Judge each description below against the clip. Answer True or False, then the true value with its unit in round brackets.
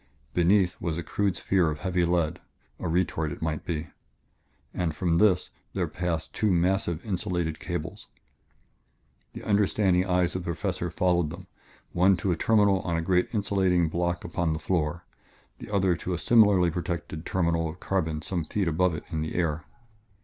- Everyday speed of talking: True (170 wpm)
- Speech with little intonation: True (2.2 semitones)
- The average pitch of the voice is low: True (90 Hz)